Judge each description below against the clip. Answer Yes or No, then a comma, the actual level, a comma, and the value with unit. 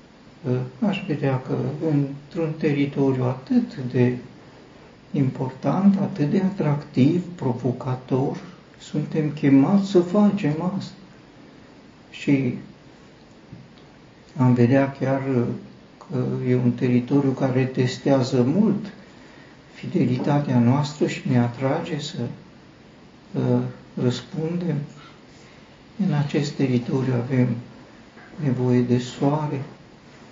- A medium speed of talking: No, slow, 85 wpm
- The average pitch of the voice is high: No, medium, 140 Hz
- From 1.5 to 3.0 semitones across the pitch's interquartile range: No, average, 4.0 semitones